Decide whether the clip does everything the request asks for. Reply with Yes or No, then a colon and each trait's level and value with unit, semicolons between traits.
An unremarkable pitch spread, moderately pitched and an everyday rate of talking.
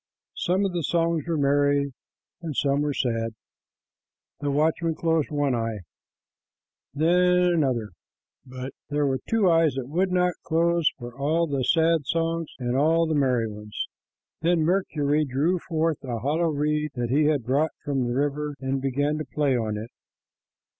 Yes: average, 3.7 semitones; medium, 145 Hz; average, 165 wpm